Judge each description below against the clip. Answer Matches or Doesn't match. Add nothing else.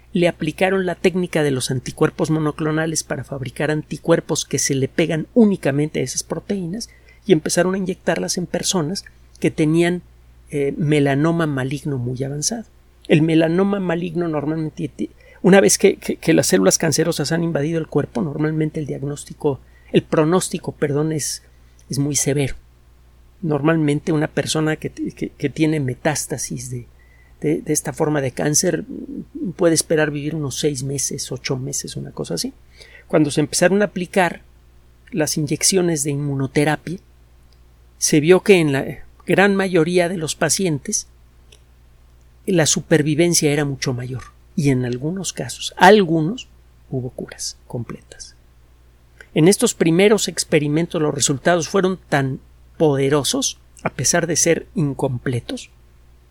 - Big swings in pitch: Doesn't match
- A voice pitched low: Doesn't match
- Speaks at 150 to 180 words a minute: Doesn't match